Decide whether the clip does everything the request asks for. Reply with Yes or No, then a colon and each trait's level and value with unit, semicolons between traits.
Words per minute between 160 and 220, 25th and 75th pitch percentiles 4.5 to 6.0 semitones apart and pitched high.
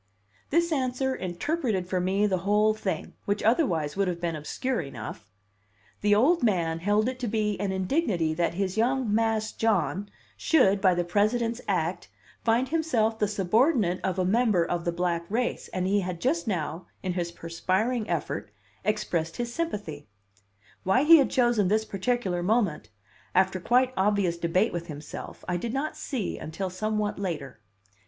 Yes: average, 165 wpm; average, 5.1 semitones; high, 205 Hz